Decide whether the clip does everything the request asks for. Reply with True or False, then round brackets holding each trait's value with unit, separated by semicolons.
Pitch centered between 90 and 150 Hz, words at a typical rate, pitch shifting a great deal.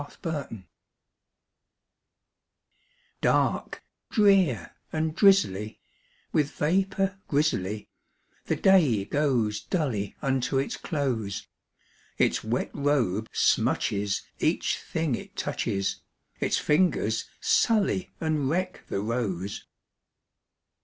False (140 Hz; 90 wpm; 7.4 semitones)